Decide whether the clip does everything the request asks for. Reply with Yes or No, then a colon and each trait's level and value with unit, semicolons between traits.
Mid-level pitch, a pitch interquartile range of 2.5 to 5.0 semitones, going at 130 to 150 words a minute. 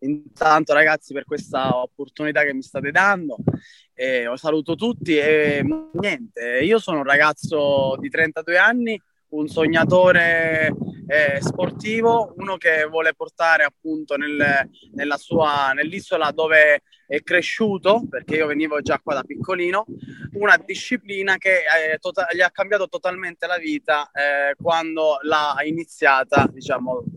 Yes: medium, 160 Hz; average, 4.0 semitones; average, 135 wpm